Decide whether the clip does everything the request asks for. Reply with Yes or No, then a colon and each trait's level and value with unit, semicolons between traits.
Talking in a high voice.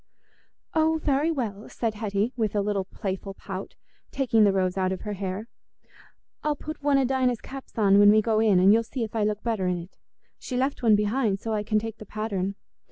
Yes: high, 215 Hz